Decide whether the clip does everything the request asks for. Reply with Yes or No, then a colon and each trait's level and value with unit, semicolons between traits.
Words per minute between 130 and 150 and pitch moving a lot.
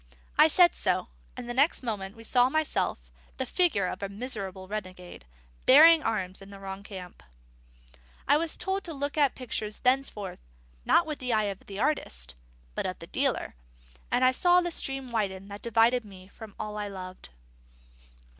No: average, 165 wpm; wide, 5.8 semitones